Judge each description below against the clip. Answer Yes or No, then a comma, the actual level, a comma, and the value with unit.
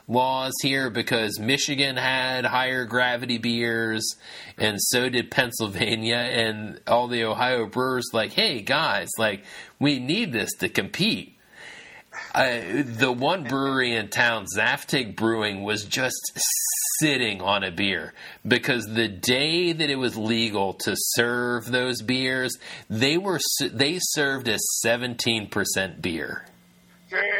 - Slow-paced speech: Yes, slow, 130 wpm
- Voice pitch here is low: Yes, low, 120 Hz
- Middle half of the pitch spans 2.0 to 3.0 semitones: Yes, narrow, 2.6 semitones